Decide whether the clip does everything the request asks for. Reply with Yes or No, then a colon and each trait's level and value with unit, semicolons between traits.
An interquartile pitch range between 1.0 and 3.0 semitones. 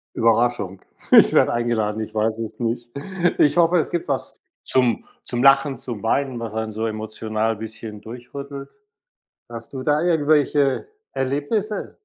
No: average, 4.0 semitones